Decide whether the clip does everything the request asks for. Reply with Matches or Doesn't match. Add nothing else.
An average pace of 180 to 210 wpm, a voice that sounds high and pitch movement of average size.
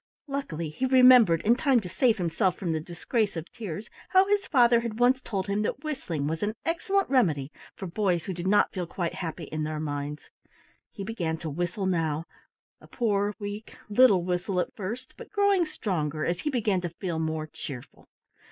Doesn't match